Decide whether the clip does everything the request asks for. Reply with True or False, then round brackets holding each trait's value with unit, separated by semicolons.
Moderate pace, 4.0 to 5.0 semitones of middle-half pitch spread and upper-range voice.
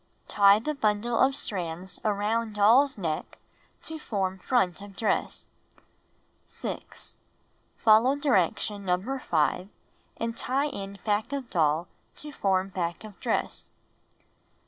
False (120 wpm; 4.3 semitones; 205 Hz)